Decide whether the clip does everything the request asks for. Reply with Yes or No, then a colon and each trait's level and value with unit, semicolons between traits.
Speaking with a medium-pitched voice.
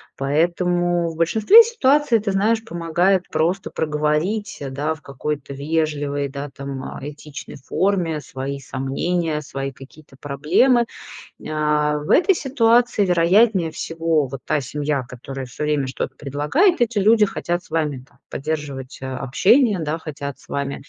Yes: medium, 155 Hz